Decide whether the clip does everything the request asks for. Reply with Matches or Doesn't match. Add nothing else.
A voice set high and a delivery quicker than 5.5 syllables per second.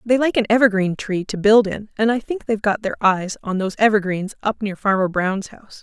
Matches